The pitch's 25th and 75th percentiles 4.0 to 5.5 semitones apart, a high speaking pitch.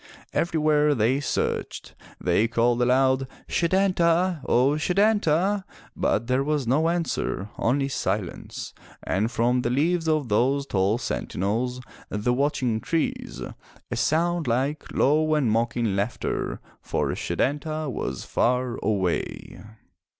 No: average, 5.0 semitones; low, 135 Hz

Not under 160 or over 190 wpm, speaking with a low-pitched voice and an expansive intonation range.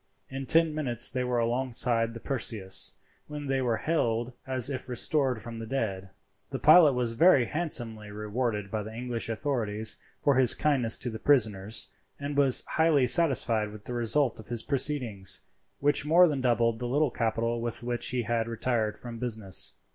No: average, 175 wpm; low, 120 Hz; average, 3.3 semitones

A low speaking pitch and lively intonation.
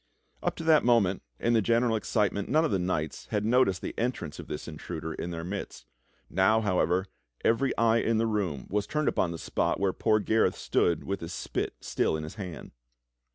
No: low, 100 Hz; average, 4.6 semitones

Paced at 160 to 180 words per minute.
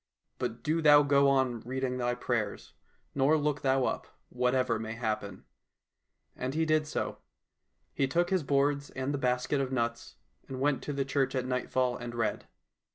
Yes: average, 170 wpm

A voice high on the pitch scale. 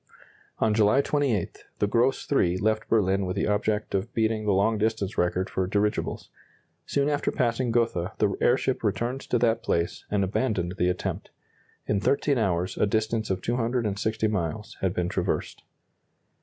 No: low, 105 Hz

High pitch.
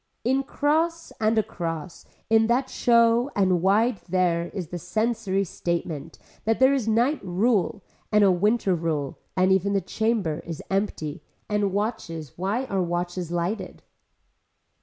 Yes: high, 195 Hz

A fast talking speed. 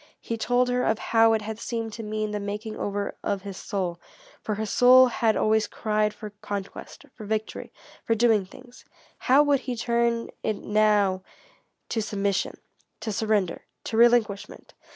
No: average, 165 wpm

